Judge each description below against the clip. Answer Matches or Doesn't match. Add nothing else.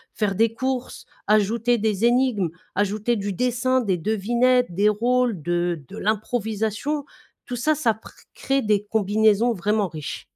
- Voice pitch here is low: Doesn't match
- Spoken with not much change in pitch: Doesn't match